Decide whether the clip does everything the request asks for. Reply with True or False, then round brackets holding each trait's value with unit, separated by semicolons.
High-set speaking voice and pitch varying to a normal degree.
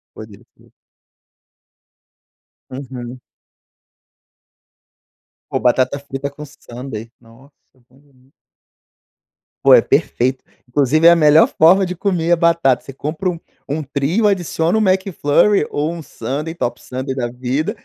False (140 Hz; 4.5 semitones)